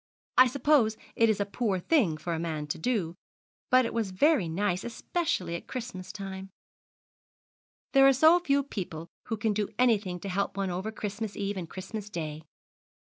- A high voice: Yes, high, 205 Hz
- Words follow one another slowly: No, average, 180 wpm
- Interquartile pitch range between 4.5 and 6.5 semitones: Yes, average, 5.1 semitones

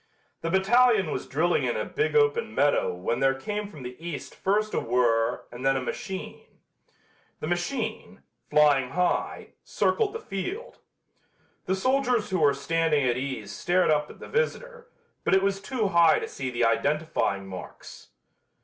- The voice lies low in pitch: No, medium, 170 Hz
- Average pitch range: No, wide, 8.1 semitones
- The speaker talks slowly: No, average, 165 wpm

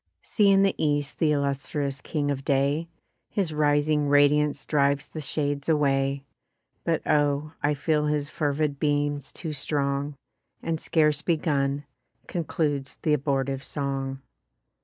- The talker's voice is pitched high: No, medium, 145 Hz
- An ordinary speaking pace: No, slow, 130 wpm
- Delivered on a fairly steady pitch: Yes, narrow, 1.5 semitones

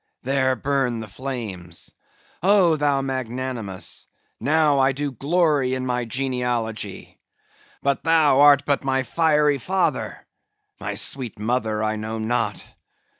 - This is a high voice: No, low, 130 Hz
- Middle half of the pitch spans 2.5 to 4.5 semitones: Yes, average, 3.6 semitones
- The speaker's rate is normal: No, slow, 125 wpm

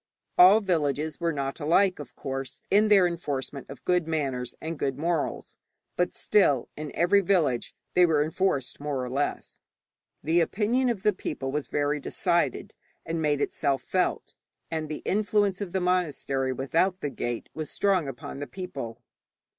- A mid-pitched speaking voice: Yes, medium, 155 Hz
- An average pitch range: Yes, average, 4.9 semitones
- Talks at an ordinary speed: Yes, average, 160 wpm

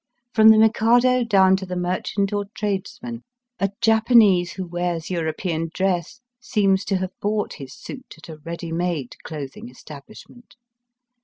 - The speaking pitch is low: No, high, 190 Hz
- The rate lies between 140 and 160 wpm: Yes, average, 145 wpm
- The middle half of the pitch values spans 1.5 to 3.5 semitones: No, average, 4.5 semitones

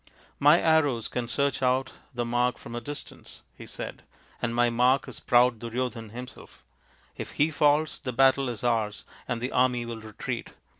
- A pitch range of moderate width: No, narrow, 2.3 semitones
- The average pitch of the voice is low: Yes, low, 125 Hz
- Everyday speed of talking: Yes, average, 180 wpm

